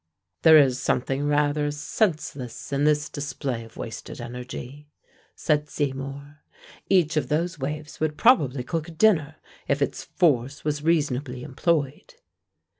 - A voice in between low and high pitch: Yes, medium, 145 Hz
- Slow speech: Yes, slow, 130 wpm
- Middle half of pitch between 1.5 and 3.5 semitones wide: Yes, narrow, 2.4 semitones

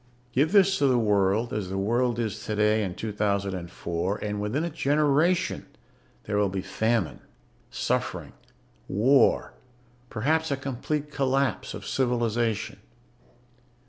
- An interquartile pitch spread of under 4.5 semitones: No, average, 5.1 semitones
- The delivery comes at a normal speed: No, slow, 120 wpm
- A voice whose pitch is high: No, low, 115 Hz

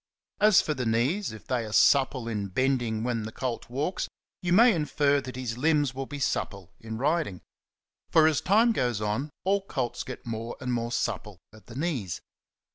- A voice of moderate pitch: No, low, 130 Hz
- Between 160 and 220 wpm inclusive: Yes, average, 190 wpm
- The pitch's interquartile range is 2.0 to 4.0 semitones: No, average, 5.2 semitones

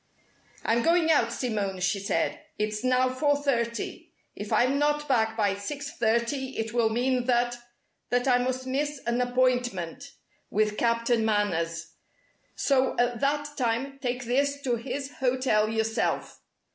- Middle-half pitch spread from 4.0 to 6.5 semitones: No, average, 3.3 semitones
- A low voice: No, high, 245 Hz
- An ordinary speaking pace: Yes, average, 145 wpm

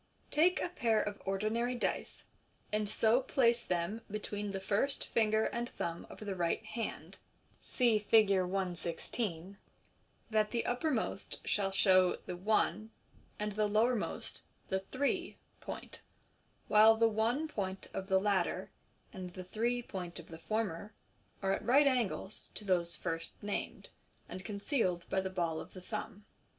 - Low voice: No, high, 210 Hz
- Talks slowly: No, average, 165 wpm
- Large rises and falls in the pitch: No, average, 3.4 semitones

